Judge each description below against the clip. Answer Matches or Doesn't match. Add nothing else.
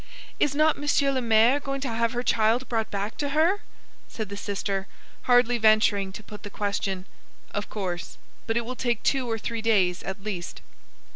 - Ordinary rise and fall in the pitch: Matches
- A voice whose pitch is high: Matches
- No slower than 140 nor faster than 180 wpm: Doesn't match